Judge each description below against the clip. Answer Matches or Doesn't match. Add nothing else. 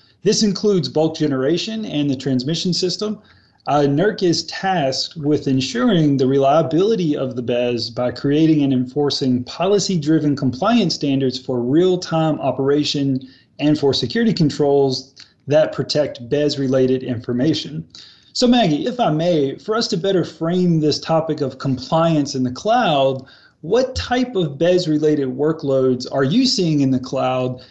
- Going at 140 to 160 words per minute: Matches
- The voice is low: Doesn't match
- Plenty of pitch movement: Doesn't match